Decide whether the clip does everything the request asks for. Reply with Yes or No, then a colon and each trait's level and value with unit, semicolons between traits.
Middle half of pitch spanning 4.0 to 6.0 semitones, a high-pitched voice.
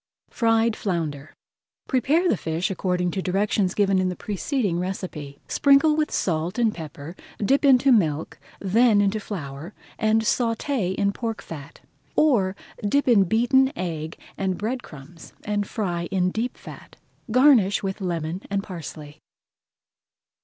Yes: average, 4.9 semitones; high, 195 Hz